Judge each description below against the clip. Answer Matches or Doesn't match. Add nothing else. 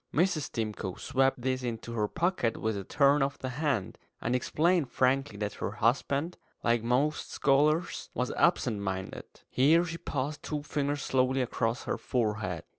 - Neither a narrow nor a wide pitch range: Matches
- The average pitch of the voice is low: Matches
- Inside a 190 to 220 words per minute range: Doesn't match